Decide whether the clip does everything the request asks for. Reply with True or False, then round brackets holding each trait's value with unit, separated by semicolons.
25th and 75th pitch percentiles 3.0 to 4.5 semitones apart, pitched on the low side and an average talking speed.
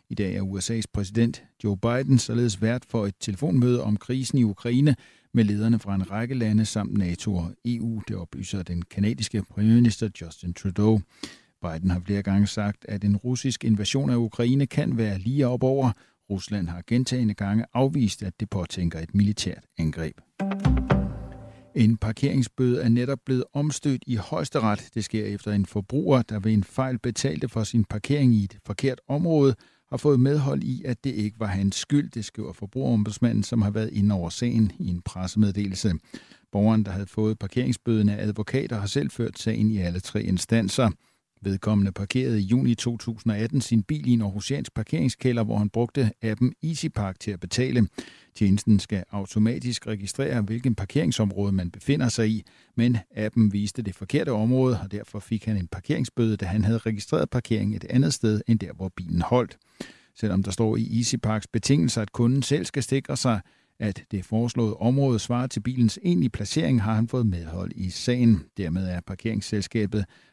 True (3.4 semitones; 110 Hz; 175 wpm)